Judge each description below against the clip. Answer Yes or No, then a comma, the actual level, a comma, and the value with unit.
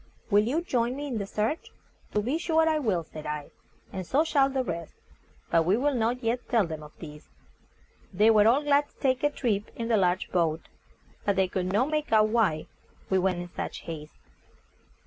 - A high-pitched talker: Yes, high, 215 Hz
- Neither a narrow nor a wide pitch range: No, wide, 6.8 semitones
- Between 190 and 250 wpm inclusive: Yes, fast, 205 wpm